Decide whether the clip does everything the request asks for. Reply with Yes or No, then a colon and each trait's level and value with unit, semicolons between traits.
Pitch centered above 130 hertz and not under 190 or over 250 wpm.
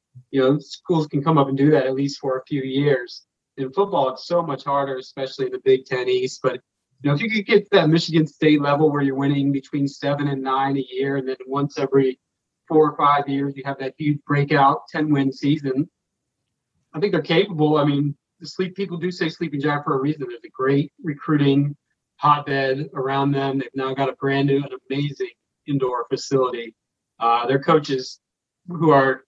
Yes: medium, 140 Hz; fast, 205 wpm